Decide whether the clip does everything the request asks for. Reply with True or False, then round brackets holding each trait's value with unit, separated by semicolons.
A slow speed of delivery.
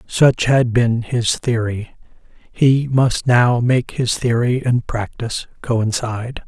True (130 wpm)